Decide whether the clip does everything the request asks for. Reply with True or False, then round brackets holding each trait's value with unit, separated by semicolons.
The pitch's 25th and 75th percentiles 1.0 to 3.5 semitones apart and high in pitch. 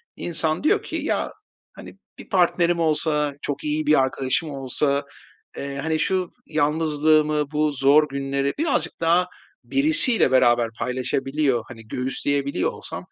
False (2.8 semitones; 150 Hz)